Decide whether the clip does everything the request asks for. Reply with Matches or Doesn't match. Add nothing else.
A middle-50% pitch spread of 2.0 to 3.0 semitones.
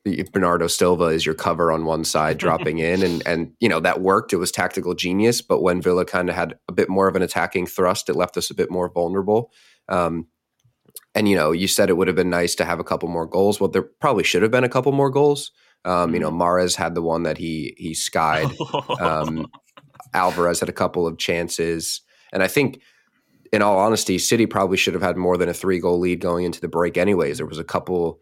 Matches